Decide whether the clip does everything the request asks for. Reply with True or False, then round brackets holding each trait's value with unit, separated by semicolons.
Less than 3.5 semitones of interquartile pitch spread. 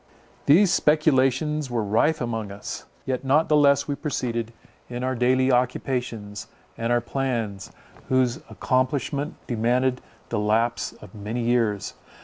True (2.8 semitones)